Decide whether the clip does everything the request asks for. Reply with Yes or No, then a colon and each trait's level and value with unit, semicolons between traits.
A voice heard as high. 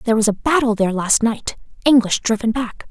Yes: high, 225 Hz